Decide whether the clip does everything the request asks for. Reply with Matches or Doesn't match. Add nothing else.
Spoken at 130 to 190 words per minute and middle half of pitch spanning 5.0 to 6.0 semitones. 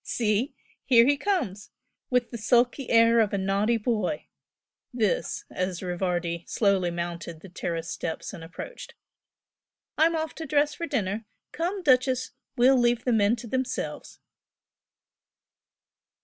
Matches